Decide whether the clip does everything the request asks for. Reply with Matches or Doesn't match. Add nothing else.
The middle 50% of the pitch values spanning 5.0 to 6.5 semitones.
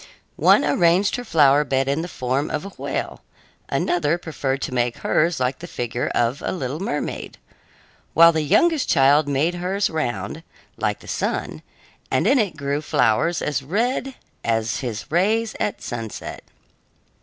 Matches